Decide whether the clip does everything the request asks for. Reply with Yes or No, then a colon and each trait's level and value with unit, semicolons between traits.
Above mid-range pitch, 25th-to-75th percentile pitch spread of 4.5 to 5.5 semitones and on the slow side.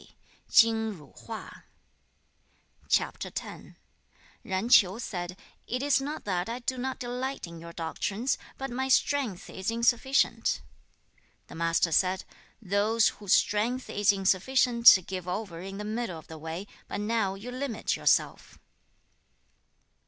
Yes: high, 210 Hz; average, 4.9 semitones; slow, 120 wpm